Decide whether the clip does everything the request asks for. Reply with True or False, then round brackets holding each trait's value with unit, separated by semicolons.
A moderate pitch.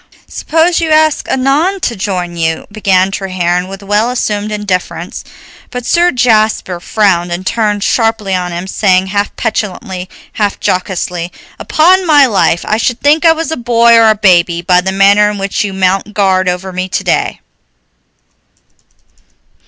False (205 Hz)